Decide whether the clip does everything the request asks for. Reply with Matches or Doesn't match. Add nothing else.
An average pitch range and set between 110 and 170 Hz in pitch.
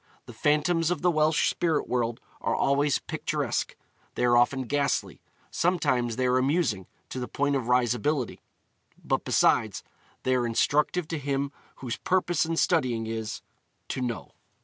Matches